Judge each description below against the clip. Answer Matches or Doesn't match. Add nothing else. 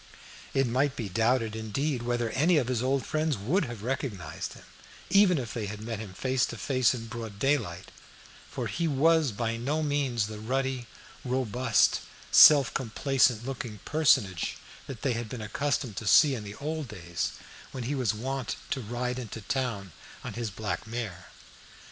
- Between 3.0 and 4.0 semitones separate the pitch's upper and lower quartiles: Matches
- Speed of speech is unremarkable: Matches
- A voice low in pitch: Matches